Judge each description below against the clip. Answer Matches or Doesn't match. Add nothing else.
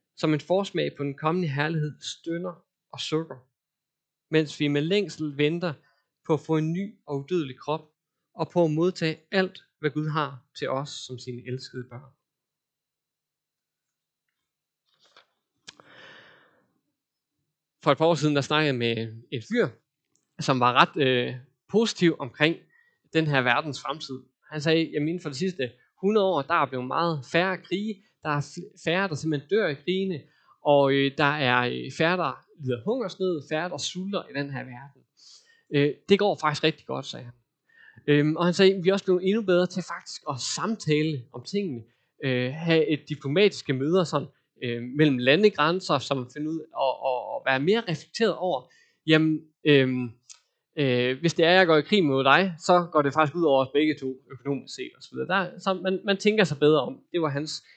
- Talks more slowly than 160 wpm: Doesn't match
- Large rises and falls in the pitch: Doesn't match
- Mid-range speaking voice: Matches